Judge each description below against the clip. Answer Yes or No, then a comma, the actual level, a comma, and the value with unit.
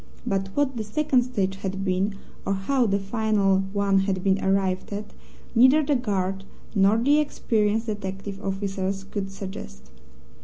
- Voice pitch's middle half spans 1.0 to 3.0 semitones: Yes, narrow, 2.5 semitones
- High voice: Yes, high, 200 Hz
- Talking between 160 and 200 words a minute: No, average, 150 wpm